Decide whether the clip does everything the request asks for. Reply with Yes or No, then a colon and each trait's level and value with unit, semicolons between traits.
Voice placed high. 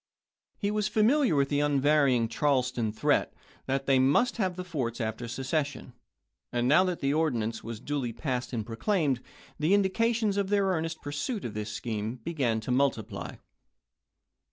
No: medium, 140 Hz